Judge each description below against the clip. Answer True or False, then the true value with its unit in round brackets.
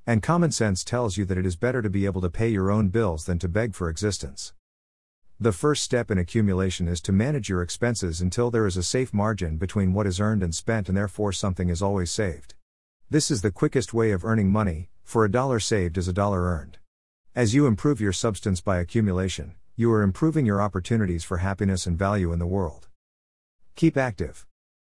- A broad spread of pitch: False (4.1 semitones)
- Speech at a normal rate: False (210 wpm)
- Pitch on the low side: True (100 Hz)